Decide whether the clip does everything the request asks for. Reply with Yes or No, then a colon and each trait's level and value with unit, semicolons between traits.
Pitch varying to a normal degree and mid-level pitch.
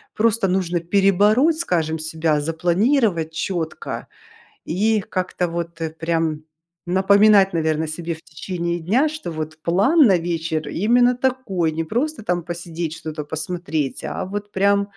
Yes: average, 4.0 semitones; medium, 175 Hz